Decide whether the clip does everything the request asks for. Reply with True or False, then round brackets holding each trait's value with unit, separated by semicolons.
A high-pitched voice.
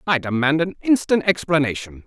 False (155 Hz)